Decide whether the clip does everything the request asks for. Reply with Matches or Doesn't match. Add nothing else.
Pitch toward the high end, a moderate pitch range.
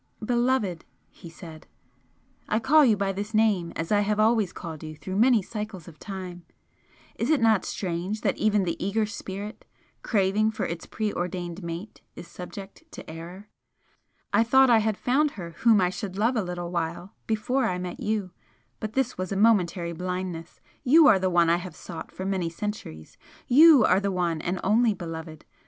Matches